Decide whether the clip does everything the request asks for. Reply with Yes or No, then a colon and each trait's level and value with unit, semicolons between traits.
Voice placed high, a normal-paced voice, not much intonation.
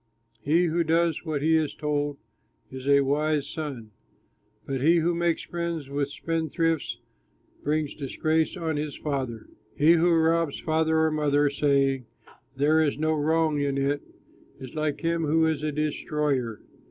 No: medium, 150 Hz; average, 155 wpm; narrow, 2.2 semitones